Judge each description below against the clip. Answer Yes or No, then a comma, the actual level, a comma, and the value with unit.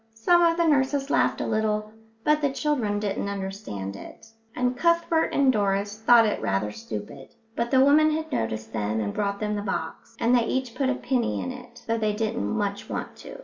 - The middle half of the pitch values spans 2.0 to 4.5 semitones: No, average, 5.1 semitones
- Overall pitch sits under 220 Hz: No, high, 225 Hz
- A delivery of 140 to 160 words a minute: No, fast, 205 wpm